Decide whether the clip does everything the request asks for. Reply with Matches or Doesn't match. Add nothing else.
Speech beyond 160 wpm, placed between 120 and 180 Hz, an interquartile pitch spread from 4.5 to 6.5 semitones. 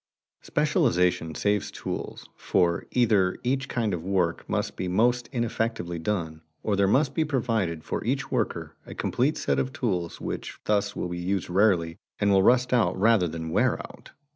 Doesn't match